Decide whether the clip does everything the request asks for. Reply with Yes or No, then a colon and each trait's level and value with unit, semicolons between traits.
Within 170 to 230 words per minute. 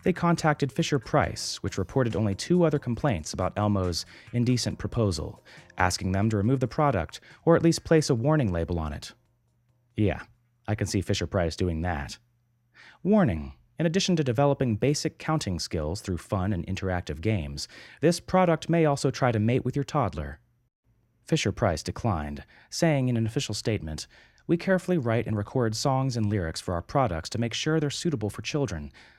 Yes: average, 175 wpm